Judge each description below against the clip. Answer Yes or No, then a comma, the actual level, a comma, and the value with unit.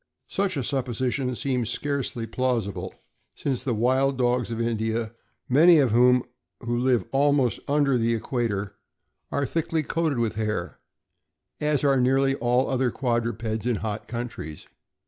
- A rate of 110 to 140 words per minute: Yes, slow, 135 wpm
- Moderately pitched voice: No, low, 125 Hz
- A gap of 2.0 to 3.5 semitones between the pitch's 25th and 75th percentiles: Yes, average, 2.9 semitones